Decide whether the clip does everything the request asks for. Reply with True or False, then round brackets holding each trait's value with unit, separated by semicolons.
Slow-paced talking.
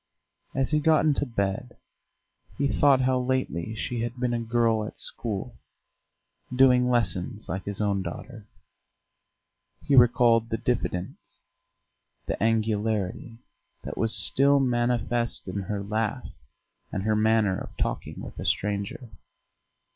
True (130 wpm)